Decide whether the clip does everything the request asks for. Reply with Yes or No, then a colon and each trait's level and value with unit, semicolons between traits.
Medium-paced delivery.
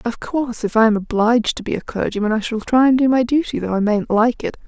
No: fast, 285 wpm